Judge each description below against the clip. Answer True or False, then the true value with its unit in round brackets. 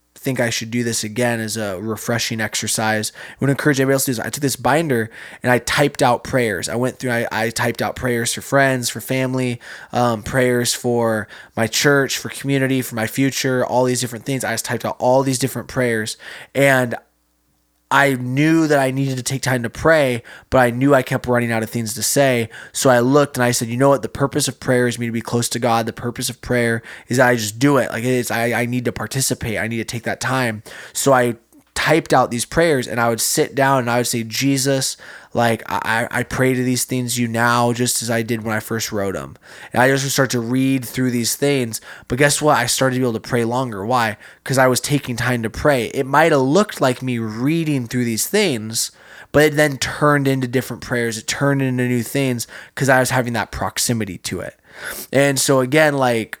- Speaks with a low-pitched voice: True (125 Hz)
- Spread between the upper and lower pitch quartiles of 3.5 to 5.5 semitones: False (2.6 semitones)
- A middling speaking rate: False (235 wpm)